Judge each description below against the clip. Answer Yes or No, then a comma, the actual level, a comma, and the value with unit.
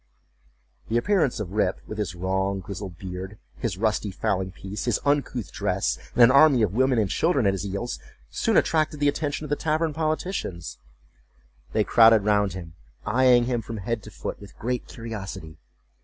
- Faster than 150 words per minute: Yes, average, 175 wpm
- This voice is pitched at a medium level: No, low, 110 Hz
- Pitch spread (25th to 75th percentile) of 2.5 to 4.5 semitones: No, average, 5.2 semitones